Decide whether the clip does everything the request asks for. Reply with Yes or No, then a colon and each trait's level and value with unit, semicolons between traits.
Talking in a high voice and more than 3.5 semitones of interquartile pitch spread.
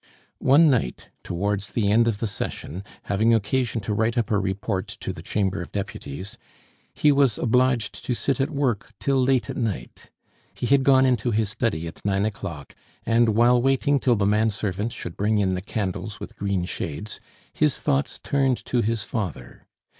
No: low, 110 Hz; average, 4.0 semitones